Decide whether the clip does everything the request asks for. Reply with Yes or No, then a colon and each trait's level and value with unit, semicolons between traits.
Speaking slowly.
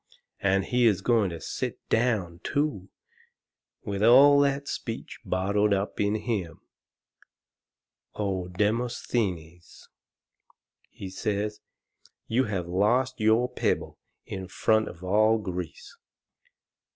Yes: slow, 105 wpm